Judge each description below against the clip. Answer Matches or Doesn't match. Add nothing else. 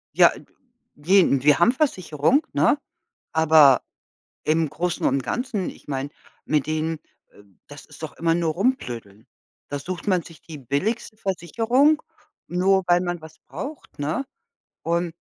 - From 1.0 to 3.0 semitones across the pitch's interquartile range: Doesn't match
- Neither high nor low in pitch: Matches